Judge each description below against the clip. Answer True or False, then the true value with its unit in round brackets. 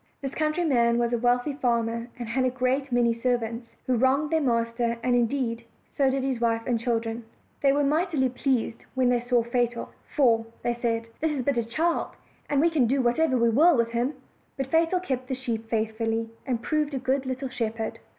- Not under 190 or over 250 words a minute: True (200 wpm)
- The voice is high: True (245 Hz)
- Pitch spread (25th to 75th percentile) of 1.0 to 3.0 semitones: True (2.7 semitones)